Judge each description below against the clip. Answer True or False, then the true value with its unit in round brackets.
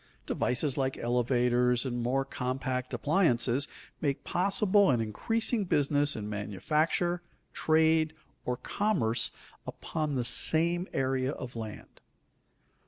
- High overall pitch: False (135 Hz)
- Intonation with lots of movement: False (4.7 semitones)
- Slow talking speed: True (105 wpm)